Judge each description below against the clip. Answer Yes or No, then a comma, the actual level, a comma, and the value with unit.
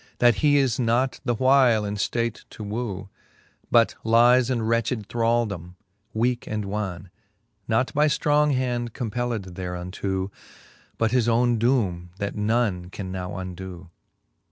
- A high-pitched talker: No, low, 115 Hz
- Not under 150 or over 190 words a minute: No, slow, 135 wpm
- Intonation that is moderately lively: Yes, average, 4.0 semitones